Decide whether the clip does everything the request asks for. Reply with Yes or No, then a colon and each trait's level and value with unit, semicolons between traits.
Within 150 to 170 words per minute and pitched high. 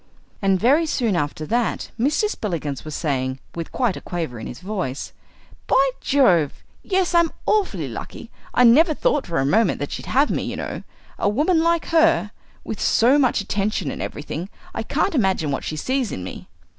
No: average, 185 wpm; high, 210 Hz